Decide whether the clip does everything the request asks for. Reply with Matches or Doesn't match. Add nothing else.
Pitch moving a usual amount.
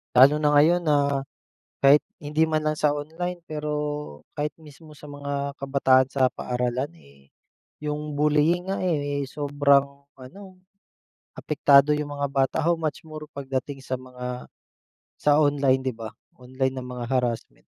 Doesn't match